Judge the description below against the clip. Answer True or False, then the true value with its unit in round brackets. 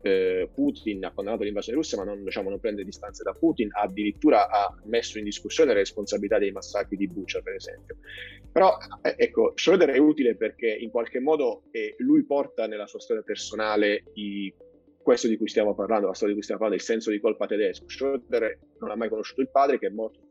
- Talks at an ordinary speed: False (205 wpm)